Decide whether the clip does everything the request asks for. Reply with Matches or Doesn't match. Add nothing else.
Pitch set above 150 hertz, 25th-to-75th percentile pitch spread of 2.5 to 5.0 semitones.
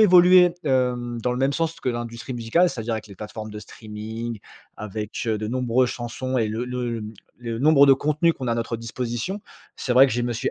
Doesn't match